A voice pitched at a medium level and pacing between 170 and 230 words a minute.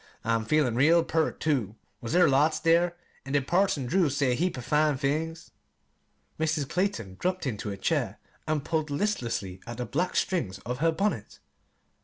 Yes: medium, 150 Hz; average, 175 wpm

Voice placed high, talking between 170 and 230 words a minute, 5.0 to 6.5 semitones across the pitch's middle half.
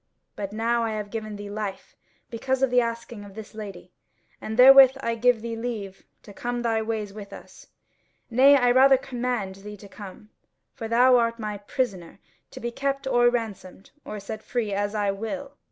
No: high, 225 Hz; average, 185 wpm; average, 3.0 semitones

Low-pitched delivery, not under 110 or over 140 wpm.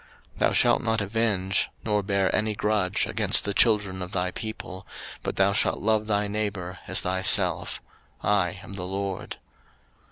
No: low, 100 Hz; average, 160 wpm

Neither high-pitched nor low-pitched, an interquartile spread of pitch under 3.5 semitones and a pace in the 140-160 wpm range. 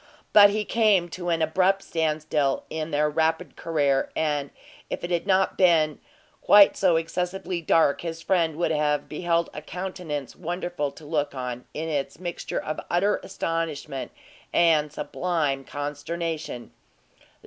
Yes: medium, 160 Hz; average, 2.9 semitones; average, 145 wpm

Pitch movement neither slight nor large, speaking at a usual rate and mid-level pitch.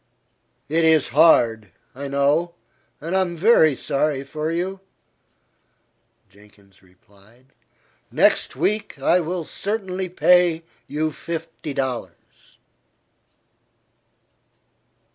No: average, 5.0 semitones; slow, 90 wpm; medium, 155 Hz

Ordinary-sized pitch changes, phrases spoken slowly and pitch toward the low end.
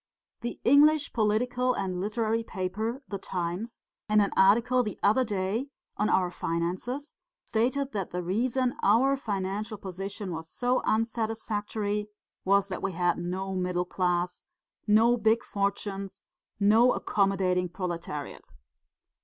No: average, 3.7 semitones; slow, 125 wpm; high, 205 Hz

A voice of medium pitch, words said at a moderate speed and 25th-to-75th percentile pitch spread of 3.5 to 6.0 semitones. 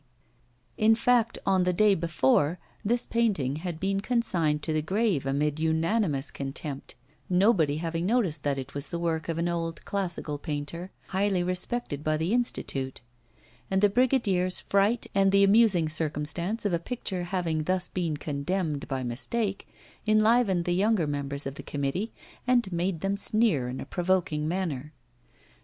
Yes: medium, 175 Hz; average, 155 wpm; average, 4.8 semitones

